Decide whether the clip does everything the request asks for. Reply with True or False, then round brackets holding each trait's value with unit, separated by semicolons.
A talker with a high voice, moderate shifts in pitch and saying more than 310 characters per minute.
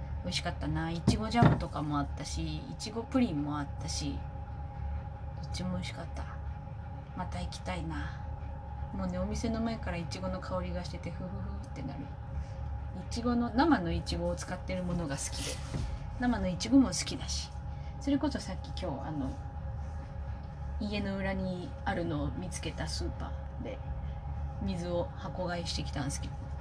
False (85 Hz; 3.9 semitones; 330 characters per minute)